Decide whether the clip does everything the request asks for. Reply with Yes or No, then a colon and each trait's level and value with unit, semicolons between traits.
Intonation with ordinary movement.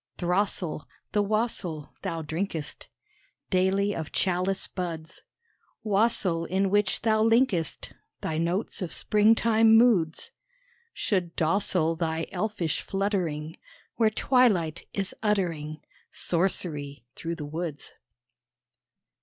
Yes: average, 4.2 semitones